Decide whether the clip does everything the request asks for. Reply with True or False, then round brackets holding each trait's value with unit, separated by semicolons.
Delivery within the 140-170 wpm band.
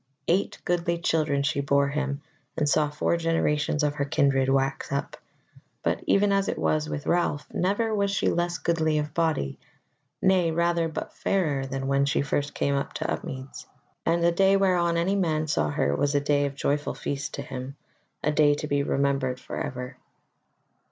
False (180 wpm)